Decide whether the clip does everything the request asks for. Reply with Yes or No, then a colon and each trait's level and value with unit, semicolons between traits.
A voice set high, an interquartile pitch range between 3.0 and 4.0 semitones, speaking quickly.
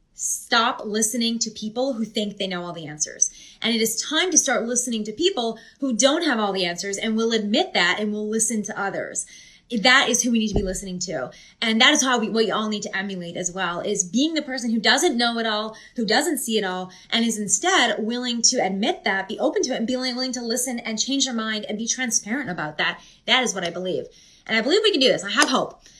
Yes: high, 225 Hz; average, 3.4 semitones; fast, 255 wpm